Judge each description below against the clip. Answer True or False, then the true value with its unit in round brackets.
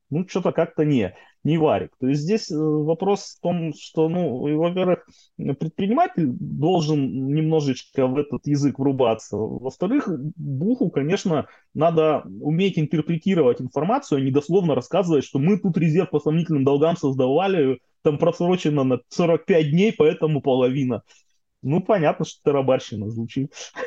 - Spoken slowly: False (135 wpm)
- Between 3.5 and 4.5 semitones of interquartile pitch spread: True (3.9 semitones)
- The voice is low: False (155 Hz)